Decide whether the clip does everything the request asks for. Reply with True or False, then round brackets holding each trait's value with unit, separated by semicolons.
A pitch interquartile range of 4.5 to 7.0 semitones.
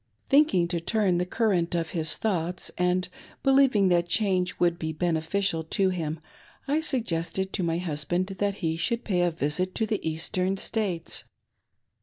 False (3.2 semitones)